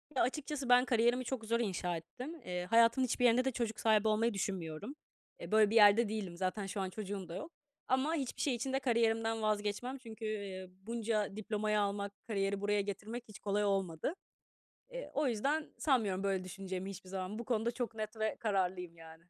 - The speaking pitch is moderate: No, high, 215 Hz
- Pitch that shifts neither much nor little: Yes, average, 3.4 semitones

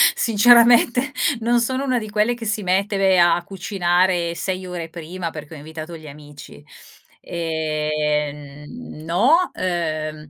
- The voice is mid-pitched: Yes, medium, 175 Hz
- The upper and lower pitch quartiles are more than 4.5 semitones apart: Yes, wide, 5.6 semitones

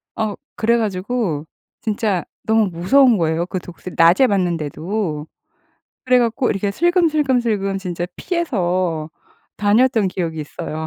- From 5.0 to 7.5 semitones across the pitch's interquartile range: Yes, wide, 5.4 semitones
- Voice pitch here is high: Yes, high, 200 Hz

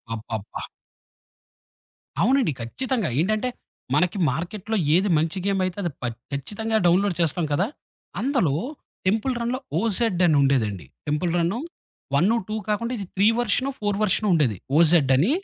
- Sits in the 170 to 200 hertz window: Yes, medium, 185 Hz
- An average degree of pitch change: No, wide, 6.1 semitones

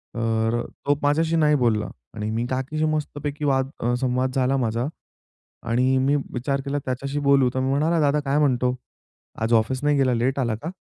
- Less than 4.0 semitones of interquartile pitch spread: Yes, average, 2.8 semitones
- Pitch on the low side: Yes, low, 130 Hz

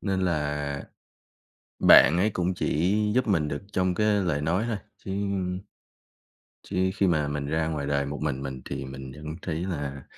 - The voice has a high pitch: No, very low, 80 Hz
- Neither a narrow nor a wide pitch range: Yes, average, 4.5 semitones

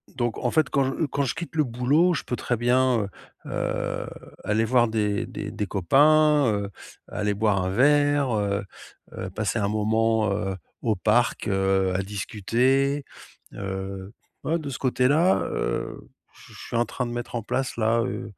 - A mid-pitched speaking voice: No, low, 115 Hz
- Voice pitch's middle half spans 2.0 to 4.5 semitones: No, average, 4.9 semitones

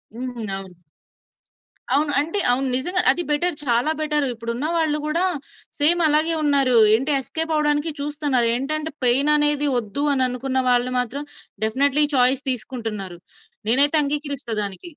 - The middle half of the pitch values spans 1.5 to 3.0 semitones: No, average, 3.4 semitones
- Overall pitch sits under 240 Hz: No, very high, 280 Hz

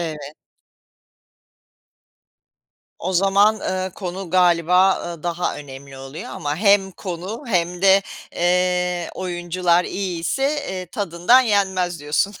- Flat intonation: Yes, narrow, 2.2 semitones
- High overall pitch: No, medium, 180 Hz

